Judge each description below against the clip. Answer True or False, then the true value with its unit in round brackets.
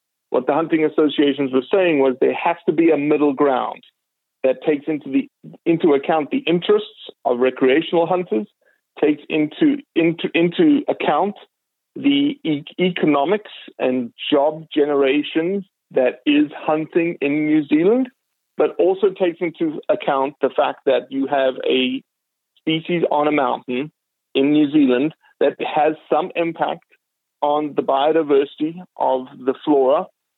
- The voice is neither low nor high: True (155 Hz)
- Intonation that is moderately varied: True (4.2 semitones)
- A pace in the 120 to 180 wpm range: True (140 wpm)